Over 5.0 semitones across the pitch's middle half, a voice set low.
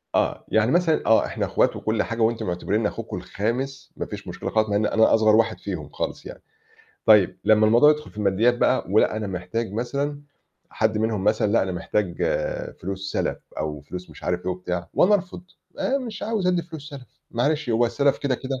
Yes: wide, 5.4 semitones; low, 110 Hz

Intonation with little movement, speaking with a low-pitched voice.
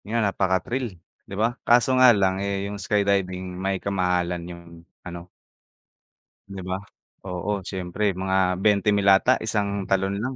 Yes: narrow, 2.2 semitones; low, 100 Hz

